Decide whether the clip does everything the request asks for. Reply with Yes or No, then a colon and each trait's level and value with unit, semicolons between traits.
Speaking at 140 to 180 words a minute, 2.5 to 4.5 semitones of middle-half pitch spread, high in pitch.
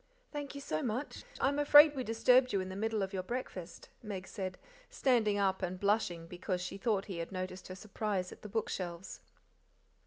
No: average, 190 wpm; average, 4.0 semitones; high, 200 Hz